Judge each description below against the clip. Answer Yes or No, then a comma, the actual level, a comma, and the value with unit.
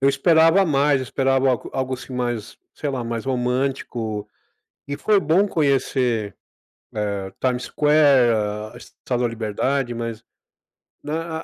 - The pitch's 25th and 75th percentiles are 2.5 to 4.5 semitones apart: Yes, average, 3.5 semitones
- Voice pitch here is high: No, low, 130 Hz